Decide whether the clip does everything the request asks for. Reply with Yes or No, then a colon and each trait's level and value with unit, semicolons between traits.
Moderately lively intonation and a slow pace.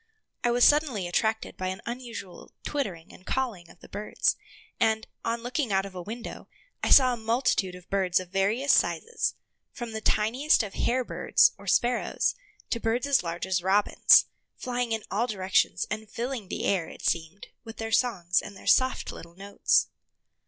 No: average, 4.5 semitones; average, 180 wpm